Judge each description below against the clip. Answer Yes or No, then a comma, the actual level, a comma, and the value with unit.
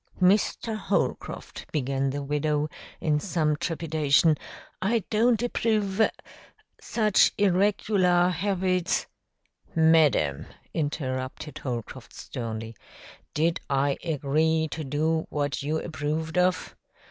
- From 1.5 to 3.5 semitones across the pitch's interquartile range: No, average, 4.2 semitones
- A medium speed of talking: No, slow, 100 wpm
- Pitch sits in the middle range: Yes, medium, 160 Hz